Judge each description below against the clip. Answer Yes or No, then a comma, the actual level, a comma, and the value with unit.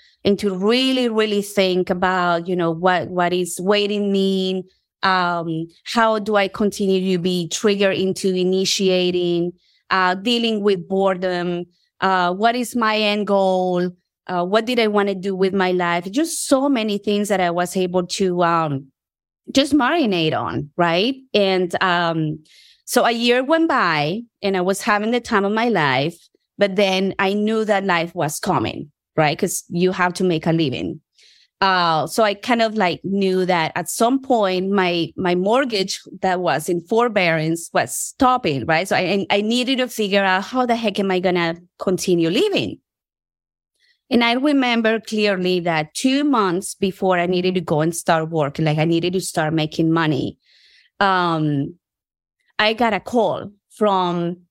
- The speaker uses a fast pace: No, average, 170 wpm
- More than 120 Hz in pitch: Yes, high, 190 Hz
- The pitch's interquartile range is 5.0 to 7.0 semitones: No, average, 3.4 semitones